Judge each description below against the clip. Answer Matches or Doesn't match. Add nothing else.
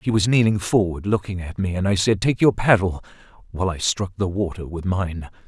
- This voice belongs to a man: Matches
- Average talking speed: Doesn't match